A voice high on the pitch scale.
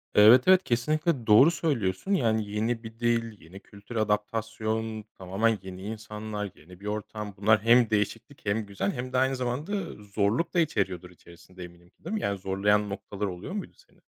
No: low, 110 Hz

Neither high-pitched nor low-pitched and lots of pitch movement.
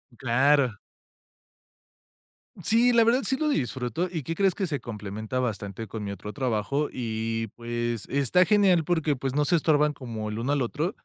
No: low, 130 Hz; wide, 6.5 semitones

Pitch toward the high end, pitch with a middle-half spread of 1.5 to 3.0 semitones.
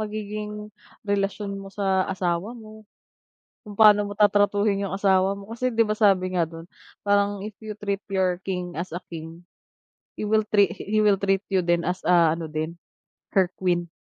Yes: high, 195 Hz; narrow, 2.6 semitones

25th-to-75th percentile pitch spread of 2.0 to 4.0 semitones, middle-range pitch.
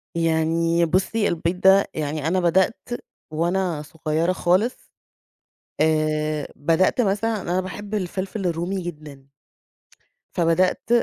Yes: average, 3.1 semitones; medium, 170 Hz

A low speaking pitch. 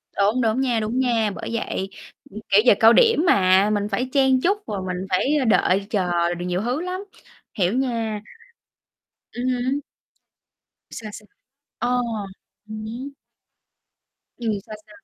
No: high, 220 Hz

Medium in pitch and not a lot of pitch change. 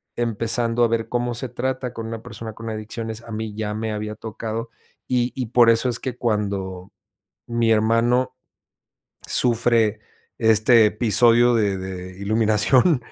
No: low, 115 Hz; narrow, 1.9 semitones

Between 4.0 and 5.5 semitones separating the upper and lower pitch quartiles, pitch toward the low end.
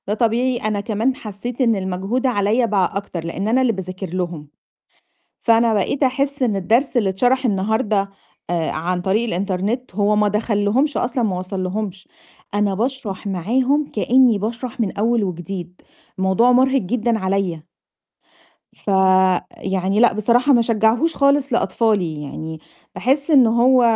No: average, 4.5 semitones; high, 215 Hz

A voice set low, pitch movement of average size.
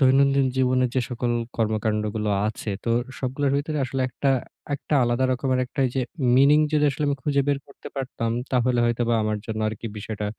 Yes: low, 130 Hz; average, 3.1 semitones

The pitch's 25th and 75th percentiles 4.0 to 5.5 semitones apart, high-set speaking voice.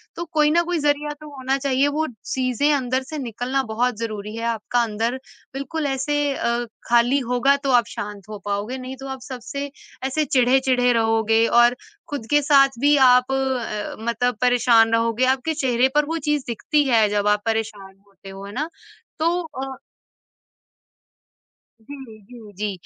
No: average, 3.6 semitones; very high, 250 Hz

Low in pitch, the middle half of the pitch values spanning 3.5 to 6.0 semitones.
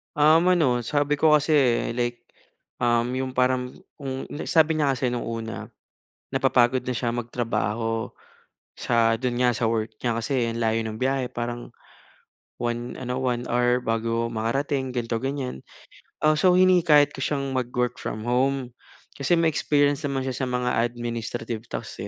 No: low, 125 Hz; average, 2.7 semitones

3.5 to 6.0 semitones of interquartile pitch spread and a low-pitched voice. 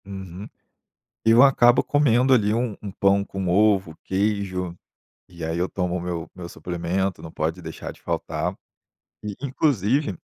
Yes: average, 3.8 semitones; very low, 95 Hz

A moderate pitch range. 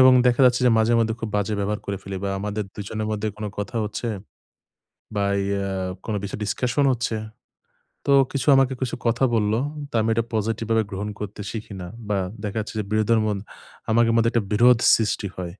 No: narrow, 2.1 semitones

